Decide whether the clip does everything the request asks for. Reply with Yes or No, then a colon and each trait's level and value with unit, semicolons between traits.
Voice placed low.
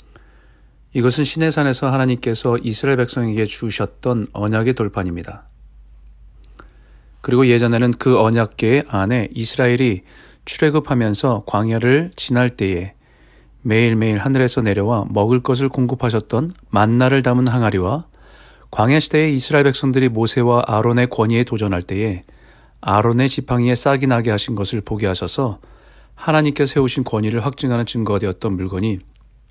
Yes: low, 120 Hz